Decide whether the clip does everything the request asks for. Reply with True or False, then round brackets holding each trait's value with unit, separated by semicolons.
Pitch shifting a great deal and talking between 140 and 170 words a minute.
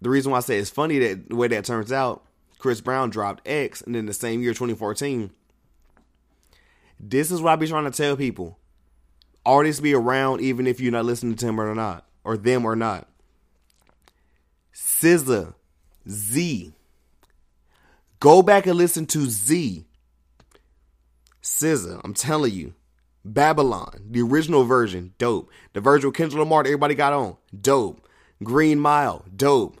True (7.9 semitones; 155 wpm)